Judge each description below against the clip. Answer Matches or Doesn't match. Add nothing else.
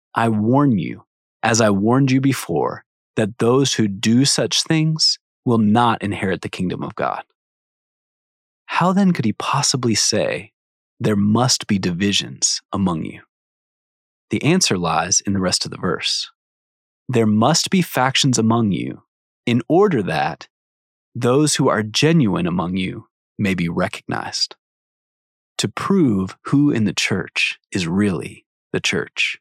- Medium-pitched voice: Doesn't match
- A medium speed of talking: Matches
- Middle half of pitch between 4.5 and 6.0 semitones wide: Matches